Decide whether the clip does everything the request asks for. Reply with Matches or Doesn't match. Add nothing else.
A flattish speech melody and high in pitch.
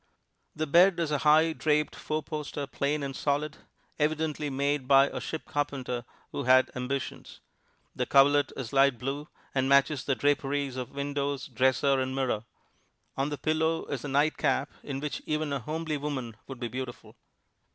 Doesn't match